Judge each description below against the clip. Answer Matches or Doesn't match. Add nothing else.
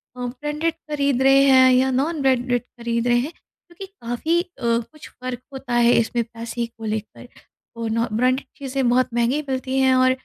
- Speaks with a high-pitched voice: Matches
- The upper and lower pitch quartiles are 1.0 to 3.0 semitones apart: Matches